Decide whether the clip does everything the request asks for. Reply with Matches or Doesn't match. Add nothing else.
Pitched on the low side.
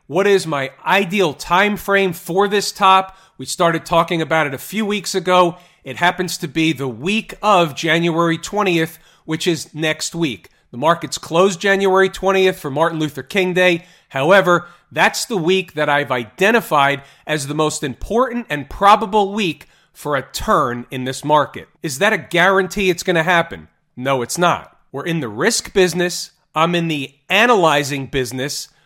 Doesn't match